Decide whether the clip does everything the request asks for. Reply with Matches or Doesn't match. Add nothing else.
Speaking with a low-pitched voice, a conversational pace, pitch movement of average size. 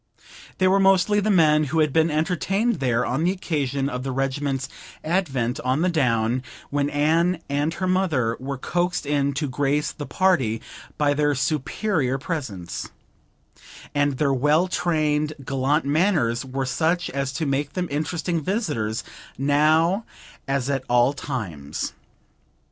Doesn't match